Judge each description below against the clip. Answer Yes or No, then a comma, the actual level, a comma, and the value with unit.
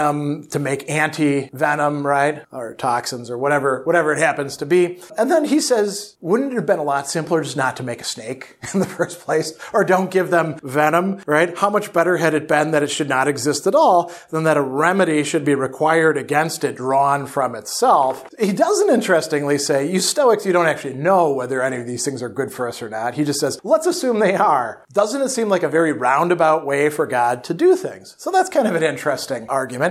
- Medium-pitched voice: Yes, medium, 155 Hz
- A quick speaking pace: Yes, fast, 225 wpm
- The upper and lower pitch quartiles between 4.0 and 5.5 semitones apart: Yes, average, 4.8 semitones